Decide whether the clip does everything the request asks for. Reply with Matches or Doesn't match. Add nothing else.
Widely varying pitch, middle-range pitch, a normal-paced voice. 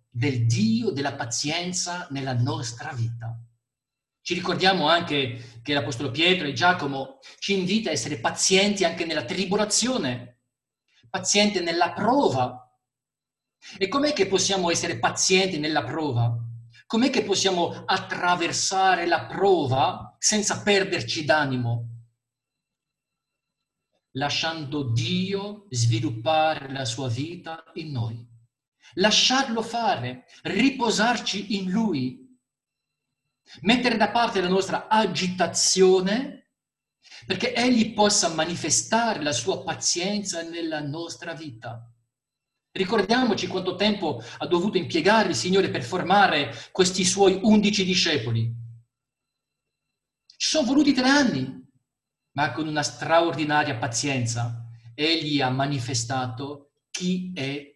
Doesn't match